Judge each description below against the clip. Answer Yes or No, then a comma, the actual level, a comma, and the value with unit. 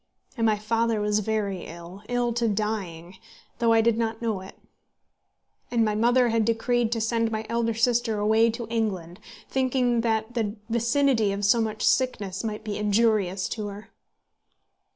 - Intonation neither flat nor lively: No, narrow, 2.0 semitones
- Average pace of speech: Yes, average, 165 wpm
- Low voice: No, high, 220 Hz